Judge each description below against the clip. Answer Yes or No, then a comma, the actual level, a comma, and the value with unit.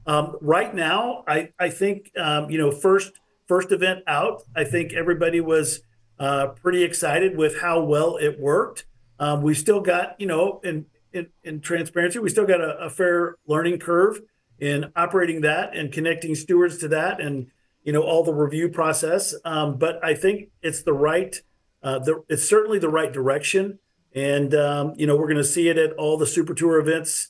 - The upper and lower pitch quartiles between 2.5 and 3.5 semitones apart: Yes, average, 2.9 semitones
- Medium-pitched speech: Yes, medium, 160 Hz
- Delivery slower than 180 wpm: No, average, 190 wpm